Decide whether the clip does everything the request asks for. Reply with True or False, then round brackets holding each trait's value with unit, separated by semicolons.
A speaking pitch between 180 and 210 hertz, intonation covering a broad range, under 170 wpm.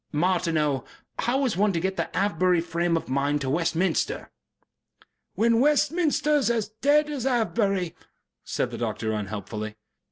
True (185 Hz; 7.8 semitones; 140 wpm)